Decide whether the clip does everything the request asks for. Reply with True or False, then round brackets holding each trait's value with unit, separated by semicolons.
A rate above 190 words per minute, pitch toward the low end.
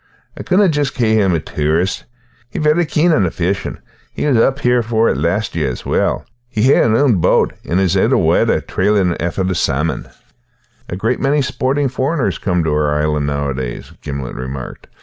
True (200 wpm; 95 Hz)